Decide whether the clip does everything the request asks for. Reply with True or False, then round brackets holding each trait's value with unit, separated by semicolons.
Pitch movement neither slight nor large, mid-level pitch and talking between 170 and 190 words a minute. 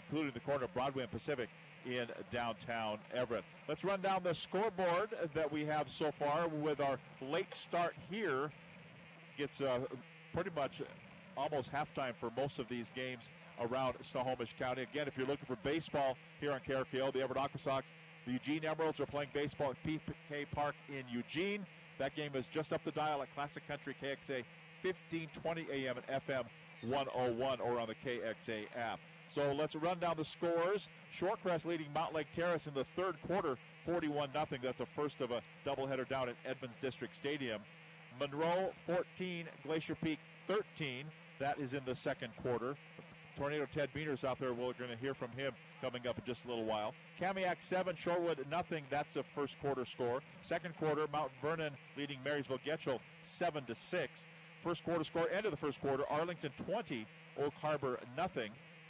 True (3.8 semitones; 150 Hz; 175 wpm)